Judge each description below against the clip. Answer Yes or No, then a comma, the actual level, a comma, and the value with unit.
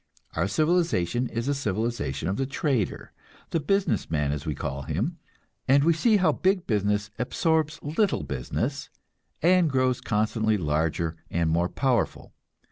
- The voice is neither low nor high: No, low, 115 Hz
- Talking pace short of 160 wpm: Yes, average, 145 wpm